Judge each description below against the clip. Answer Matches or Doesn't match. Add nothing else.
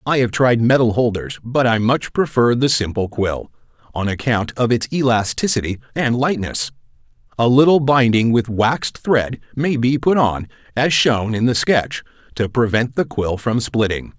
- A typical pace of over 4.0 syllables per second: Matches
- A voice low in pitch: Matches